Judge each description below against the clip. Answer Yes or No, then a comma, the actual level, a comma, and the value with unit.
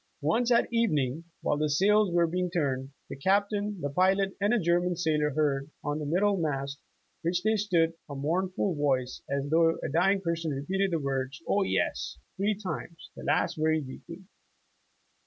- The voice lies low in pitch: No, medium, 165 Hz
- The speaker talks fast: No, average, 175 wpm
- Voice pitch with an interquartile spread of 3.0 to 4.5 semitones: No, average, 4.9 semitones